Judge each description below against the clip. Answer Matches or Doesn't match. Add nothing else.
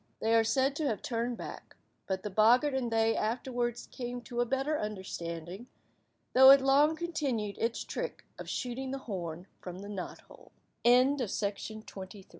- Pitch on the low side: Doesn't match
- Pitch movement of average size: Matches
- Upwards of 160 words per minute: Doesn't match